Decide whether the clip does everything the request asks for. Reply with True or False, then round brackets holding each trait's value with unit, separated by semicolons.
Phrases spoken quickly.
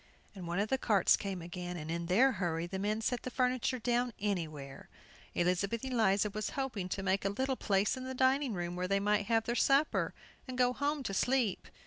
True (210 wpm)